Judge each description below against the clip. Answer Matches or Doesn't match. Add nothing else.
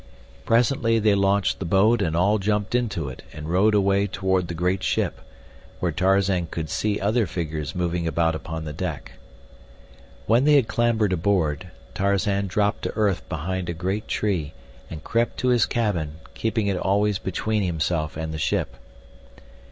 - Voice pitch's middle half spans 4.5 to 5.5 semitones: Doesn't match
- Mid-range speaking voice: Doesn't match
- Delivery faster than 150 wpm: Matches